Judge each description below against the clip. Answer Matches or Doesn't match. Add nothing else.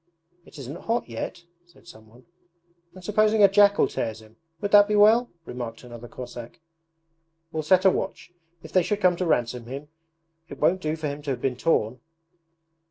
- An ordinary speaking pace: Matches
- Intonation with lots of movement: Matches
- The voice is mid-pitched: Matches